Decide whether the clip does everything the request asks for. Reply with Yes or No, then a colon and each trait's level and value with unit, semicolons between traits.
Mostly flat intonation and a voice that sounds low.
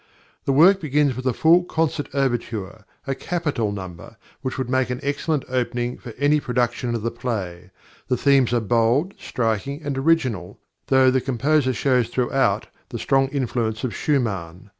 No: average, 3.5 semitones; low, 130 Hz